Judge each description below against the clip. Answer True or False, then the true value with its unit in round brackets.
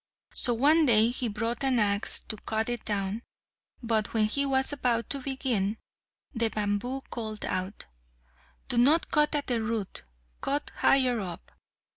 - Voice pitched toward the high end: True (230 Hz)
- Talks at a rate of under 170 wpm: True (155 wpm)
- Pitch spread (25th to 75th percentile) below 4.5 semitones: True (3.7 semitones)